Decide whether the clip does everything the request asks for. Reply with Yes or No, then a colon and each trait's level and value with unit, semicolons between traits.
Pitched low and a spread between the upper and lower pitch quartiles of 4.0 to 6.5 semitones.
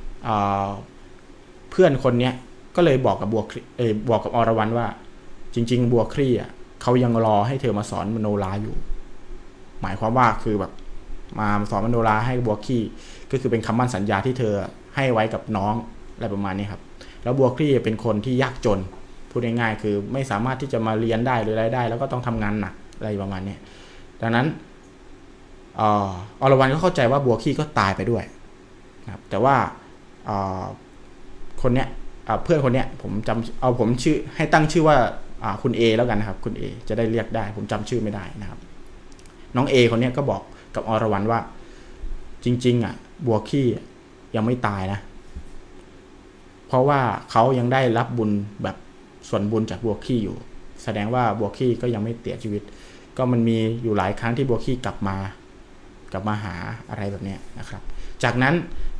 No: low, 115 Hz; average, 3.4 semitones